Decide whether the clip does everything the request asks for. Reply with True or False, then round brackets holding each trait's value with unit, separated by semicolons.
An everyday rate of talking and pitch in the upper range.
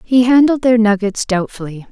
True (155 wpm; 225 Hz)